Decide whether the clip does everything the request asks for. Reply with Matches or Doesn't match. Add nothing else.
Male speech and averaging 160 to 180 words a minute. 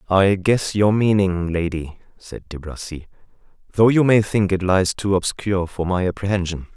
Matches